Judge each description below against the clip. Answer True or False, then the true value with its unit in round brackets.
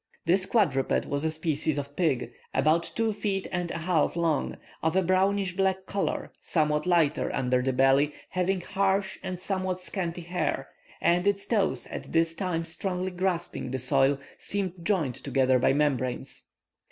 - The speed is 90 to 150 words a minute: False (160 wpm)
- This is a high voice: False (170 Hz)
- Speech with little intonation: False (4.5 semitones)